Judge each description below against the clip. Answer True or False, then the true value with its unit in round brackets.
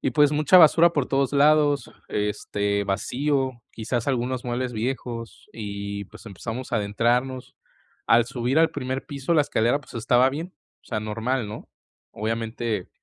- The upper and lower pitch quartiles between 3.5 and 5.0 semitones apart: True (3.9 semitones)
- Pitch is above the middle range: False (125 Hz)